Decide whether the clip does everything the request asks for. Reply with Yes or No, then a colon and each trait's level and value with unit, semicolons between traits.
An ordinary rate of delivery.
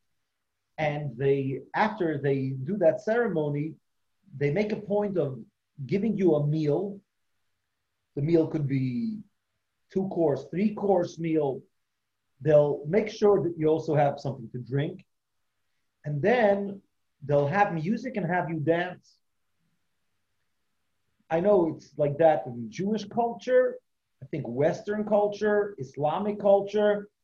No: slow, 130 wpm